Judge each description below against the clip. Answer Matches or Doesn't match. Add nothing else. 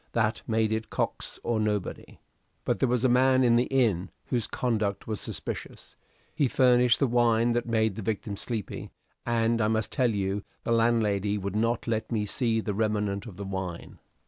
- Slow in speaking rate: Doesn't match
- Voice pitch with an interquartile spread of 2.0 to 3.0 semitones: Matches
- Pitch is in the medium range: Doesn't match